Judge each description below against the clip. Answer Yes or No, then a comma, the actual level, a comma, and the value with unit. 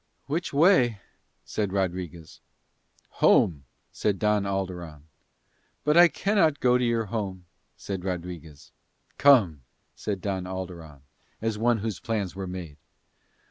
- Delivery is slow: Yes, slow, 120 wpm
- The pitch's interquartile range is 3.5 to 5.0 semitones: Yes, average, 4.7 semitones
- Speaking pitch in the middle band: No, very low, 95 Hz